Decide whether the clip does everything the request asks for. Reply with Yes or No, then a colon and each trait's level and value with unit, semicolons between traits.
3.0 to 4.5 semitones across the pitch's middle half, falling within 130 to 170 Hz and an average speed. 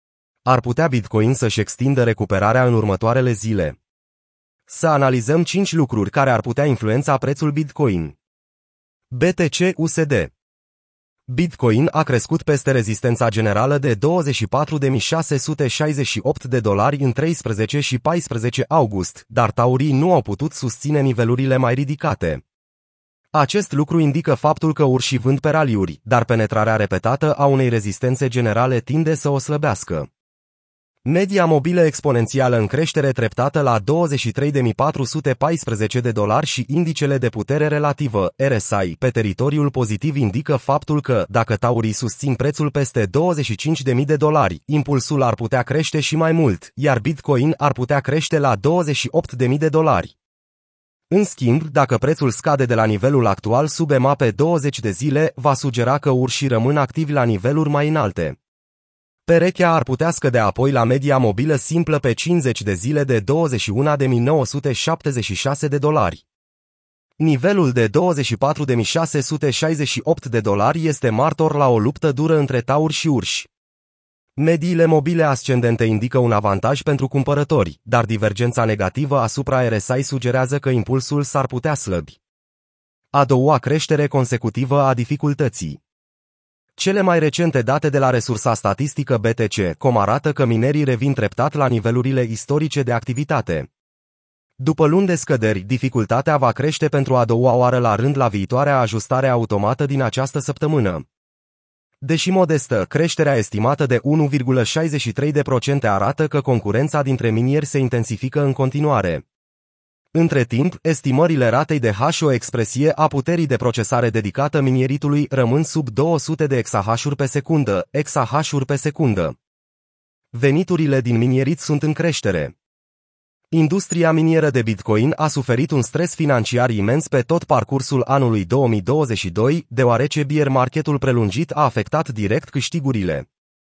Yes: average, 4.2 semitones; low, 135 Hz; average, 135 wpm